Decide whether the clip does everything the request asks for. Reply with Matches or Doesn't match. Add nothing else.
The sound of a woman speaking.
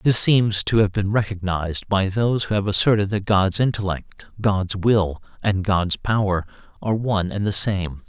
Doesn't match